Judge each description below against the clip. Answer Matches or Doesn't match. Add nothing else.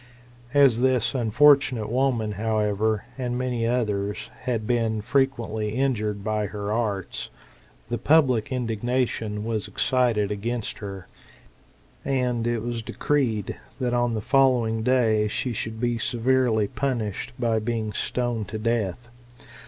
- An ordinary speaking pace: Doesn't match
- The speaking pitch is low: Matches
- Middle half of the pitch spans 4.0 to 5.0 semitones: Doesn't match